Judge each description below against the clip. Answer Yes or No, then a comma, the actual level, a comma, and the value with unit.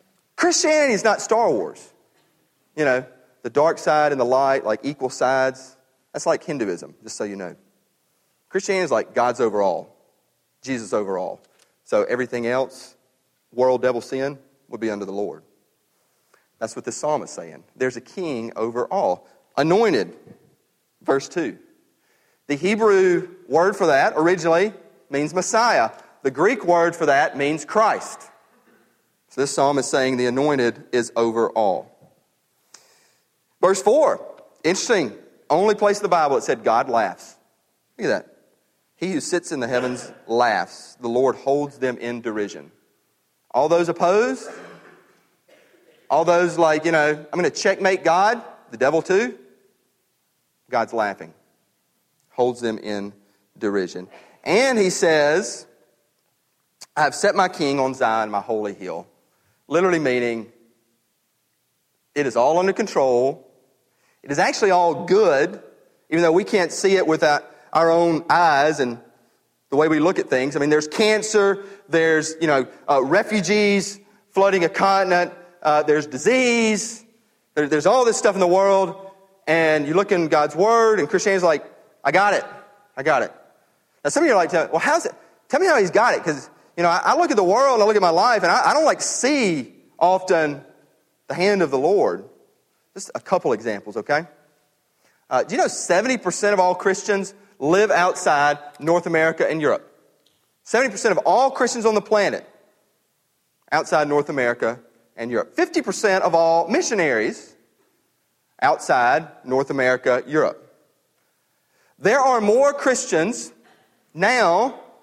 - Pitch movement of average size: No, wide, 7.2 semitones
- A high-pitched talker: No, medium, 155 Hz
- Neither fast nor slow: Yes, average, 150 wpm